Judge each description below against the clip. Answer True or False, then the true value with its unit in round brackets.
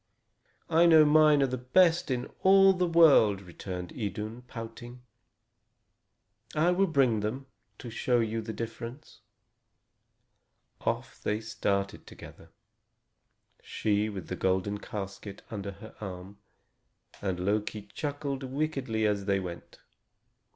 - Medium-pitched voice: False (115 Hz)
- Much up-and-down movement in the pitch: True (5.8 semitones)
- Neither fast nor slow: False (120 wpm)